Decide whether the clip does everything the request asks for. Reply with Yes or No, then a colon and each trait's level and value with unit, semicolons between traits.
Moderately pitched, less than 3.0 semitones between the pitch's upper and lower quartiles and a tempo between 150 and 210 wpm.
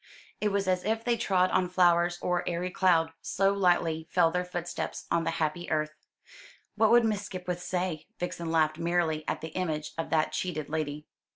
Yes: medium, 175 Hz; narrow, 2.4 semitones; average, 185 wpm